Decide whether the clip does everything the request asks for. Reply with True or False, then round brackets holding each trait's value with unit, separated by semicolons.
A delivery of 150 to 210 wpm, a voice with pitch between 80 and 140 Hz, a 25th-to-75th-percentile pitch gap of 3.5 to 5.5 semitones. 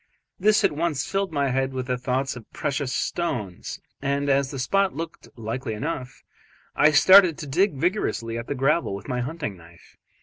True (175 wpm; 135 Hz; 4.7 semitones)